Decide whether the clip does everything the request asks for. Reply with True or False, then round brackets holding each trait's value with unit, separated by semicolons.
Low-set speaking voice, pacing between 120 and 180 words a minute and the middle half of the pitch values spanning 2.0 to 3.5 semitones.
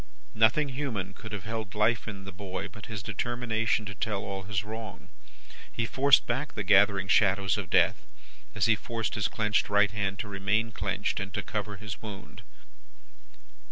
True (105 Hz; 175 wpm; 2.4 semitones)